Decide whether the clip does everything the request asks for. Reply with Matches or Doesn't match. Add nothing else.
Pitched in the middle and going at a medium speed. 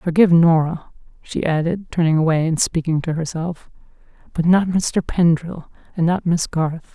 Matches